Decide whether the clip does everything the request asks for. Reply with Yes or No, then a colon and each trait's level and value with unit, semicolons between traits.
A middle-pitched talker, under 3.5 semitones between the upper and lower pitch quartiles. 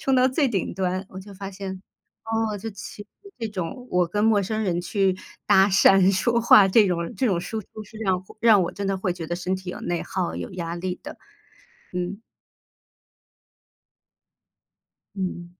No: high, 195 Hz; average, 3.0 semitones